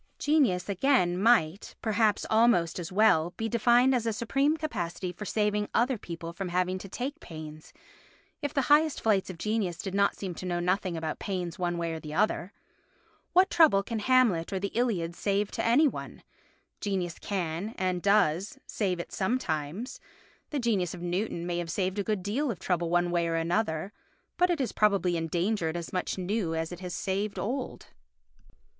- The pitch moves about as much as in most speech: Yes, average, 4.5 semitones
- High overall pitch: Yes, high, 195 Hz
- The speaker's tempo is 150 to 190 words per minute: Yes, average, 185 wpm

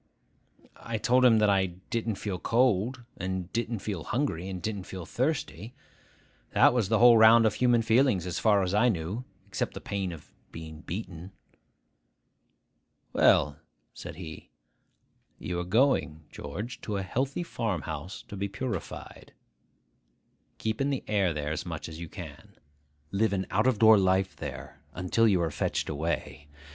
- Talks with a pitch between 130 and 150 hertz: No, low, 100 Hz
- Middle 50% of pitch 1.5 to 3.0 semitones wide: No, average, 4.5 semitones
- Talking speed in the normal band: Yes, average, 160 wpm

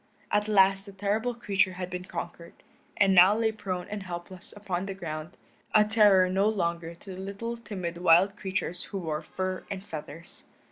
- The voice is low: No, high, 190 Hz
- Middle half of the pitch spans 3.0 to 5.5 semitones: No, narrow, 2.6 semitones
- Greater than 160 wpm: Yes, average, 180 wpm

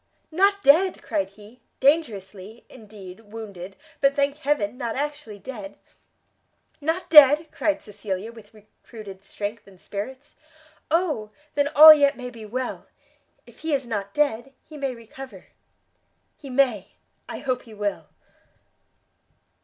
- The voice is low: No, high, 245 Hz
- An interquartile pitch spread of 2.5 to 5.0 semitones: No, wide, 5.6 semitones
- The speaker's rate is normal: No, slow, 130 wpm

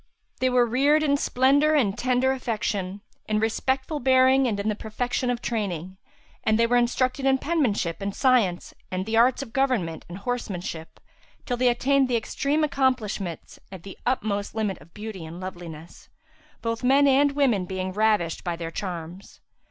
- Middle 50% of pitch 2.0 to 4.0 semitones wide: No, wide, 5.5 semitones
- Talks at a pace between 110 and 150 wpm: No, average, 165 wpm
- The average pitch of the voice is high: Yes, high, 230 Hz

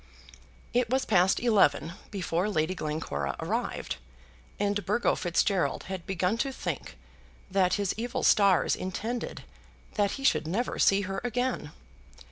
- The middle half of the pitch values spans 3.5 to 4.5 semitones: Yes, average, 4.2 semitones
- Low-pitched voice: No, high, 195 Hz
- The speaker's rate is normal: No, slow, 130 wpm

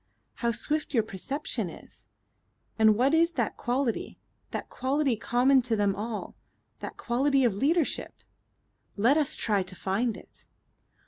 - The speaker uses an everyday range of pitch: Yes, average, 4.2 semitones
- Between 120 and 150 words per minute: Yes, average, 140 wpm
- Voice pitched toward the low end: No, high, 245 Hz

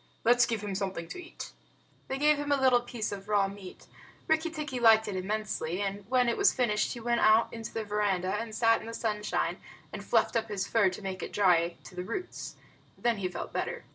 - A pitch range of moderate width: Yes, average, 3.6 semitones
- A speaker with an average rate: No, fast, 225 wpm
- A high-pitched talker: Yes, high, 215 Hz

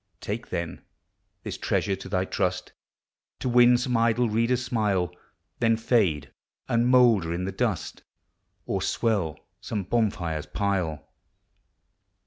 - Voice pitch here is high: No, low, 105 Hz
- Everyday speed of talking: No, slow, 120 wpm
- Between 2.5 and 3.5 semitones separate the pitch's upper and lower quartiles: No, average, 4.8 semitones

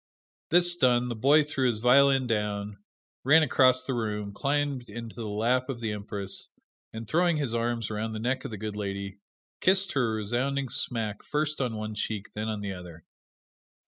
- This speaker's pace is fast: No, average, 185 wpm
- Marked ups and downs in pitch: No, average, 4.2 semitones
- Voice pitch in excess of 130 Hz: No, low, 115 Hz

